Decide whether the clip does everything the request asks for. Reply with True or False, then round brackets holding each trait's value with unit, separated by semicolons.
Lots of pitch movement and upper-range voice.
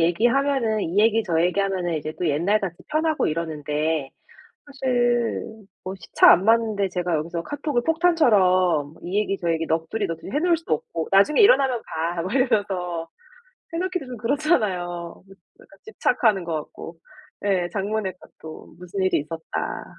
True (6.2 semitones; 195 Hz)